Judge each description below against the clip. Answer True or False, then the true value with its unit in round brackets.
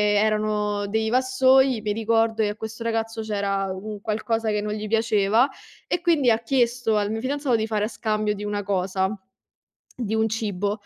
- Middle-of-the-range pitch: False (220 Hz)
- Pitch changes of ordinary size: False (1.7 semitones)